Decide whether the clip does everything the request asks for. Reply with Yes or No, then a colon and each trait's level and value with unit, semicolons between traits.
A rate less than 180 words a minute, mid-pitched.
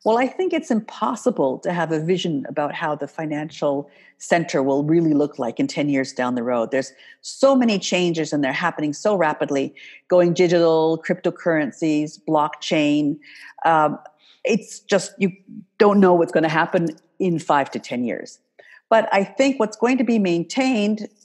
Yes: average, 170 wpm; medium, 170 Hz